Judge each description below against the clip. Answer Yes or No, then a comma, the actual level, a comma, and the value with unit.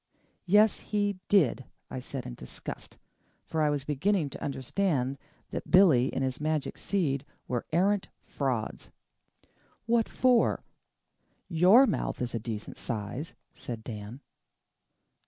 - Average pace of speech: No, slow, 125 wpm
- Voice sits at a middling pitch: Yes, medium, 145 Hz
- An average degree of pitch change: No, wide, 7.6 semitones